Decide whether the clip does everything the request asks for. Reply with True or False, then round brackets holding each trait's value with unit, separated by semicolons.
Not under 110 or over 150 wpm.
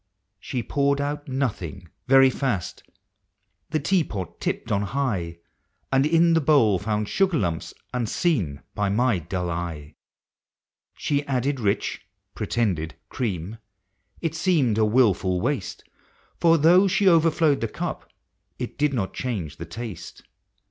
True (140 wpm)